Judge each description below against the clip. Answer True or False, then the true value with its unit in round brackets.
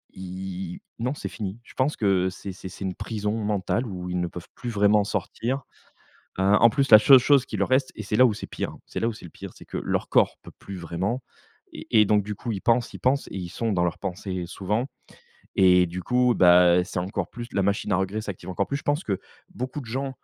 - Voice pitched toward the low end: True (105 Hz)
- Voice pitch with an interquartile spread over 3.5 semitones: True (4.2 semitones)